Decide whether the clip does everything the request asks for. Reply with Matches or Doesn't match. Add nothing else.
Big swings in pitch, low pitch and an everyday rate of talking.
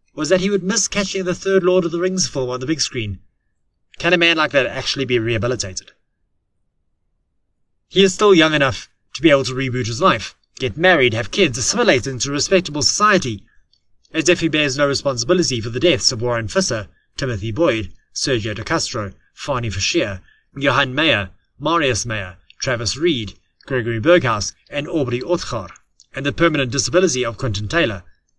Matches